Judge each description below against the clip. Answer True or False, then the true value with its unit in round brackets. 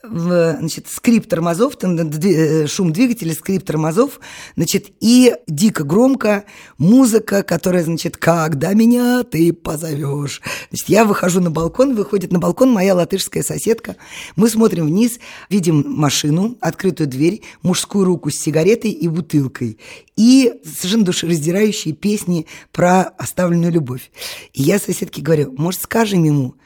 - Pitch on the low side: False (180 Hz)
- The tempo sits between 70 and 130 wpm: True (125 wpm)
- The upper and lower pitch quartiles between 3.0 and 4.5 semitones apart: False (4.9 semitones)